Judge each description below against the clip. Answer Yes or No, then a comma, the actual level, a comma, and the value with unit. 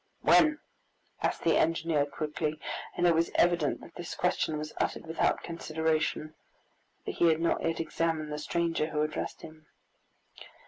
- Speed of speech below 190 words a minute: Yes, average, 150 wpm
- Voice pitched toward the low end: No, medium, 160 Hz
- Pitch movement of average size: No, narrow, 1.5 semitones